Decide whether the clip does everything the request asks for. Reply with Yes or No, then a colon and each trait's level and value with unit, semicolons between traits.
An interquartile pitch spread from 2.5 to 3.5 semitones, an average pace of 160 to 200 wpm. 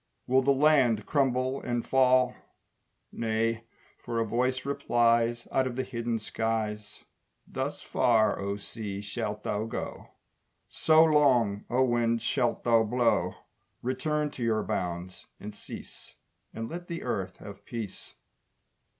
No: average, 3.1 semitones; slow, 135 wpm